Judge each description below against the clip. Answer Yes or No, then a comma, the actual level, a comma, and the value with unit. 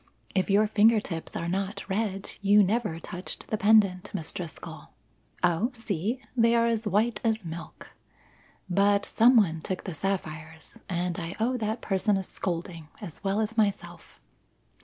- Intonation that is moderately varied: Yes, average, 3.6 semitones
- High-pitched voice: Yes, high, 200 Hz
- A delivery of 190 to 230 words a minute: No, average, 160 wpm